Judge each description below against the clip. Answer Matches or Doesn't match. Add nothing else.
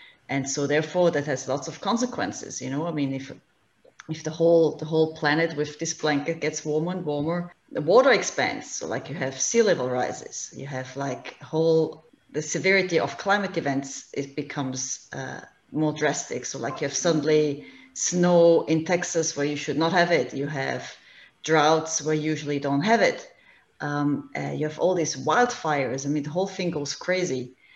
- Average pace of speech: Matches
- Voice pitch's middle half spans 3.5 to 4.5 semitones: Doesn't match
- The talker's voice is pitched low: Doesn't match